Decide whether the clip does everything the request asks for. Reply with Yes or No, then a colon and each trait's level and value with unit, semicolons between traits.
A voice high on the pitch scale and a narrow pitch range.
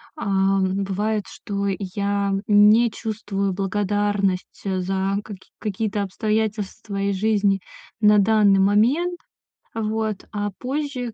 Yes: high, 205 Hz; narrow, 1.8 semitones